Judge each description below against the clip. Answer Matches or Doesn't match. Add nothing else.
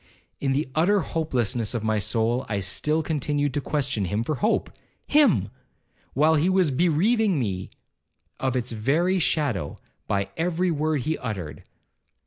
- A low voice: Doesn't match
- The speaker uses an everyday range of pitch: Doesn't match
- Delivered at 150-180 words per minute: Doesn't match